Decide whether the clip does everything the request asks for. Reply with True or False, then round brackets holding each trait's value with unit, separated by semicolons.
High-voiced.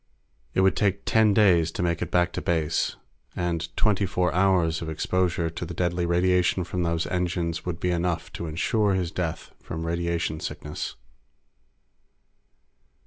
False (85 Hz)